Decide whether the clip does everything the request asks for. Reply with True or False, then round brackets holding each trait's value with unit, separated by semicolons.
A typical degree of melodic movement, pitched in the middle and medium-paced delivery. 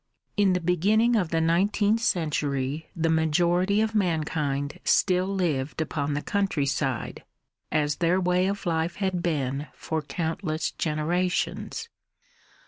False (3.7 semitones; 170 Hz; 125 wpm)